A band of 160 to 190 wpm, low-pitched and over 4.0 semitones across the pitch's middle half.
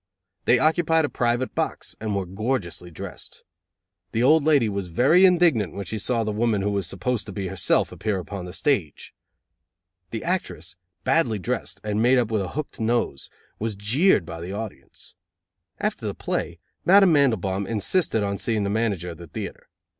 Yes: average, 175 wpm; low, 110 Hz; average, 5.0 semitones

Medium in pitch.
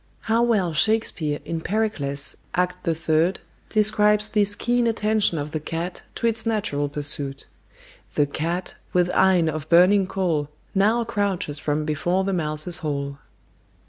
Yes: medium, 180 Hz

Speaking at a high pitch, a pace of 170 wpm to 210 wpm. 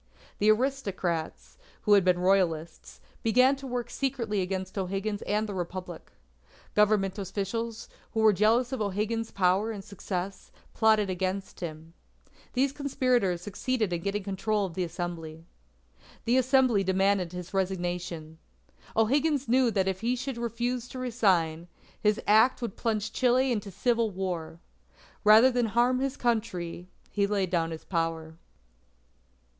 No: high, 205 Hz; average, 140 wpm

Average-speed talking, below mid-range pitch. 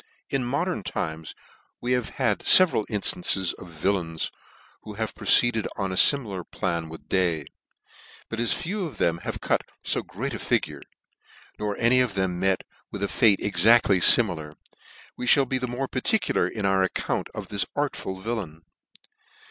Yes: average, 165 wpm; low, 105 Hz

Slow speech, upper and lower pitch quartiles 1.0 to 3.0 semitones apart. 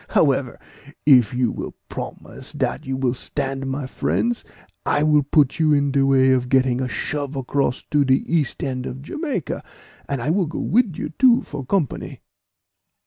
No: average, 175 wpm; narrow, 2.6 semitones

